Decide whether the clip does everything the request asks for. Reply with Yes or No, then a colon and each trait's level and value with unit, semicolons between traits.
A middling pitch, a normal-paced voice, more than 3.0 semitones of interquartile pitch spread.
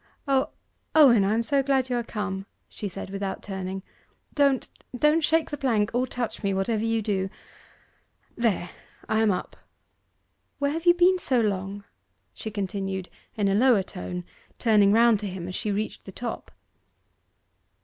No: high, 215 Hz; average, 165 wpm; average, 4.7 semitones